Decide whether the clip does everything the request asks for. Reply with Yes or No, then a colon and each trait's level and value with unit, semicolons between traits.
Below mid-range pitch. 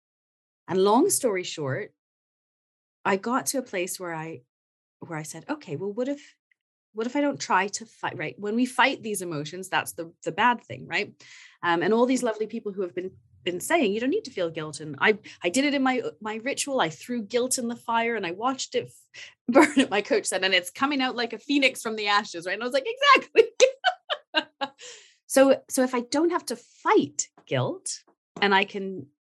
No: high, 235 Hz